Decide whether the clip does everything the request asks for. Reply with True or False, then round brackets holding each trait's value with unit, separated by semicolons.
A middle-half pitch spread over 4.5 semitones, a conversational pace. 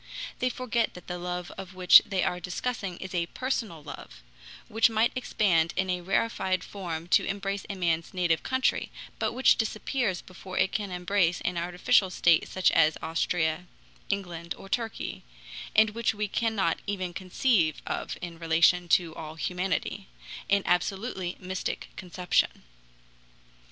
False (2.8 semitones; 145 wpm)